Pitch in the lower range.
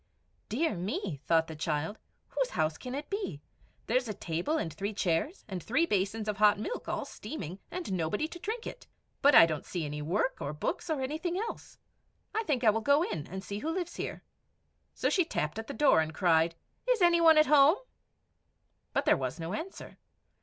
No: high, 220 Hz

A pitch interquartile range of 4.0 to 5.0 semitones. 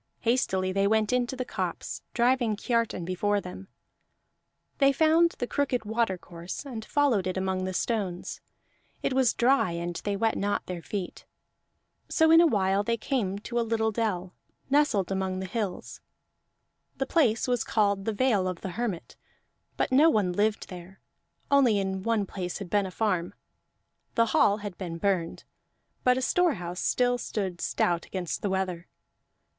Yes: average, 4.5 semitones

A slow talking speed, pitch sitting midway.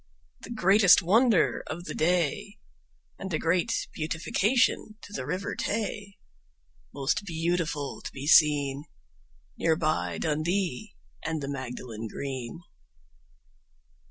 Yes: slow, 110 wpm; medium, 165 Hz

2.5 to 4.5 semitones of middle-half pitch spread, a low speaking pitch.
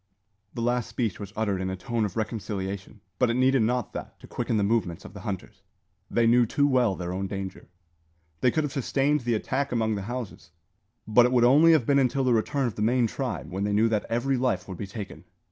Yes: average, 3.8 semitones; low, 115 Hz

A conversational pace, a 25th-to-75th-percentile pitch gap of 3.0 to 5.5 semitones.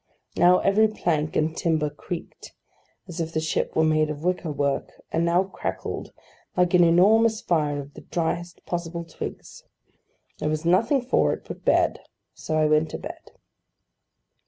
No: average, 160 wpm; narrow, 2.6 semitones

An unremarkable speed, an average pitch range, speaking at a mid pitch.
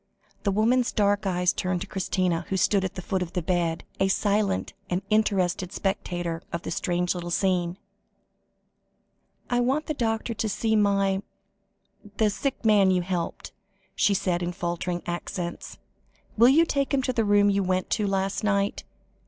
No: average, 170 wpm; average, 3.0 semitones; high, 195 Hz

